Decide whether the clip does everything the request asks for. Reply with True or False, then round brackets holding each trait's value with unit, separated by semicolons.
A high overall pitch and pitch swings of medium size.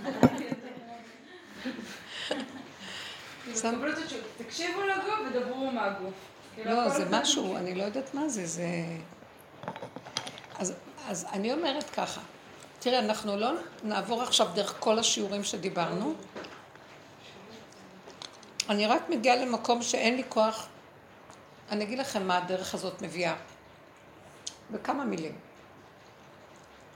True (230 Hz; 4.2 semitones)